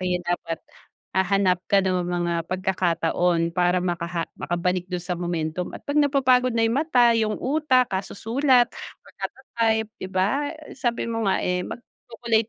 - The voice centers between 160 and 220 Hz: Yes, high, 190 Hz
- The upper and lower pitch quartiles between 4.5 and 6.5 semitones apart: Yes, average, 5.1 semitones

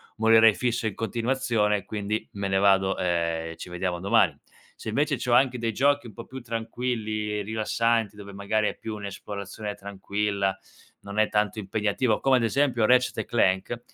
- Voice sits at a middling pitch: No, low, 105 Hz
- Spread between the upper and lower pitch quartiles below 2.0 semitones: No, average, 2.7 semitones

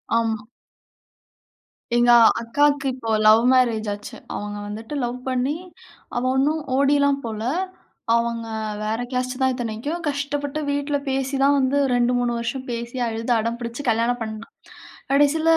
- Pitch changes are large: No, average, 3.5 semitones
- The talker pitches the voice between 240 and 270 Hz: Yes, high, 245 Hz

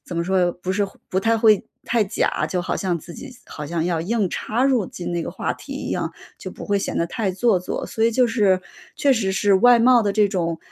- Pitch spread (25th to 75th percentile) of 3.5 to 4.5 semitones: Yes, average, 4.2 semitones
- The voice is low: No, high, 195 Hz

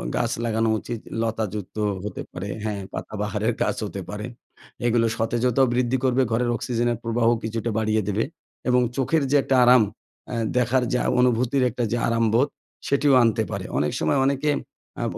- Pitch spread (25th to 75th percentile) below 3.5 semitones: Yes, narrow, 2.4 semitones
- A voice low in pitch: Yes, low, 115 Hz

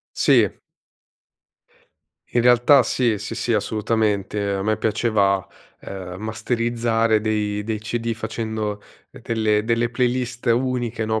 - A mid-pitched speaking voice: No, low, 110 Hz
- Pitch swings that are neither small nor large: No, narrow, 1.9 semitones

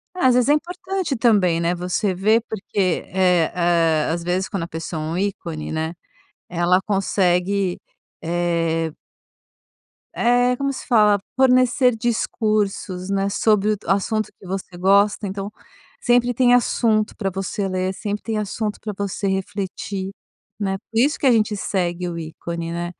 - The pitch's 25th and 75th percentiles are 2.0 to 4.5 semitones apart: Yes, average, 3.7 semitones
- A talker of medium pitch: No, high, 195 Hz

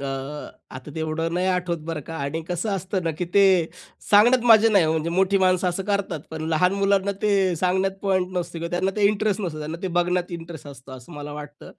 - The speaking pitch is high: No, medium, 180 Hz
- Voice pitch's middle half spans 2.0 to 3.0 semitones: No, average, 3.4 semitones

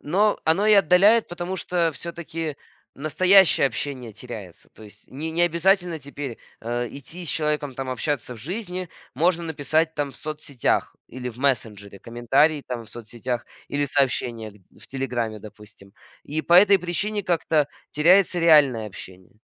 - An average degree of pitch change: No, wide, 6.1 semitones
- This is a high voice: No, medium, 145 Hz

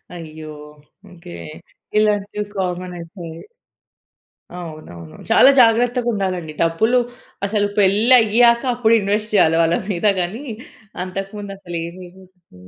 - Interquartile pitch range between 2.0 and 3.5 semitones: No, average, 4.0 semitones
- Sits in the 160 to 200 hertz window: Yes, high, 190 Hz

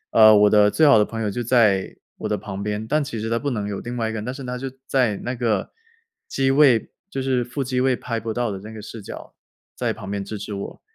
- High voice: No, low, 115 Hz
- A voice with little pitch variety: No, average, 3.3 semitones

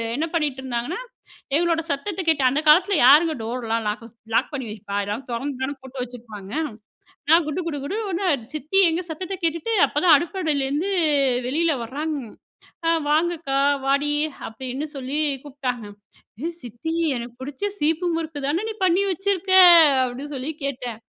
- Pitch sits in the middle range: No, very high, 290 Hz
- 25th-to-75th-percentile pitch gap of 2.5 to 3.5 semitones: No, average, 4.7 semitones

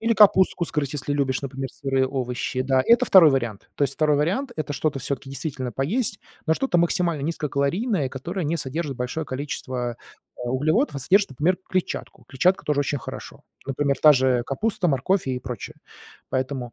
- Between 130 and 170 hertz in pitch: Yes, medium, 140 Hz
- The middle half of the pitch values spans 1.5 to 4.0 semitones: No, average, 4.5 semitones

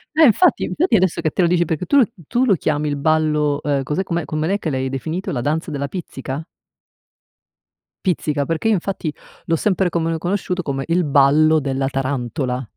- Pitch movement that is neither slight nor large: Yes, average, 4.2 semitones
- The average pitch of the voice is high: No, medium, 155 Hz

